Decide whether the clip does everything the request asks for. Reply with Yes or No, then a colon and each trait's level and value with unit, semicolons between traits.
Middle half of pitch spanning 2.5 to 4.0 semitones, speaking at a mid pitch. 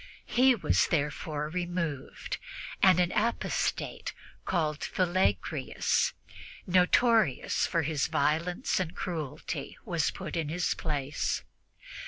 Yes: average, 3.4 semitones; medium, 170 Hz